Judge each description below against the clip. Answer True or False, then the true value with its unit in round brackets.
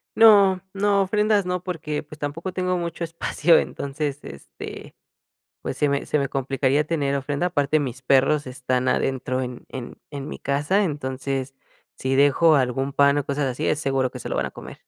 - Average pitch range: True (3.9 semitones)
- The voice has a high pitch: False (145 Hz)